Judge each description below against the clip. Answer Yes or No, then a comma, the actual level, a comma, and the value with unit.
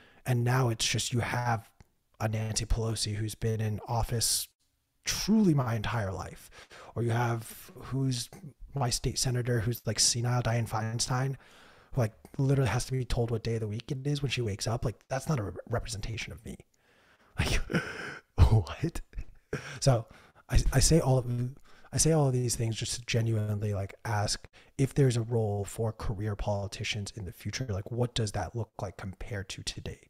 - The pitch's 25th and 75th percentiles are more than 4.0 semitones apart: No, average, 3.0 semitones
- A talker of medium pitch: No, low, 115 Hz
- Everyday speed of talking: Yes, average, 185 wpm